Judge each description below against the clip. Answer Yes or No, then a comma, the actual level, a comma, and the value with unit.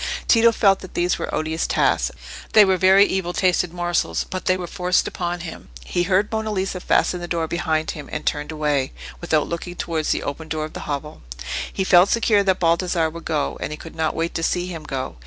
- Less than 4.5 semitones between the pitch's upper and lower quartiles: Yes, average, 2.8 semitones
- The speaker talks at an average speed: No, fast, 220 wpm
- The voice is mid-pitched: Yes, medium, 175 Hz